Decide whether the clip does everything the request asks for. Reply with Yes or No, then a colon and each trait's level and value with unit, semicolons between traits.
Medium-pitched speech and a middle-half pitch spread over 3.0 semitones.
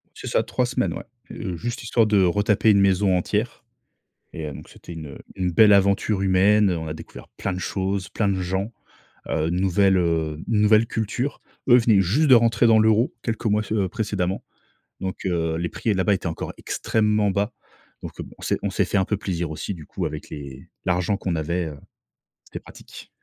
No: low, 100 Hz; average, 3.4 semitones